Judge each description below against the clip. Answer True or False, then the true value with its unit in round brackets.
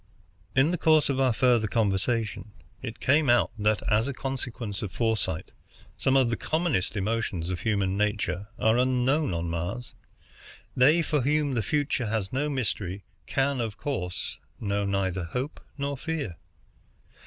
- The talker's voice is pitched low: True (115 Hz)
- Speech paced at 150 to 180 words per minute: True (155 wpm)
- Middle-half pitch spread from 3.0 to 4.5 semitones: False (5.0 semitones)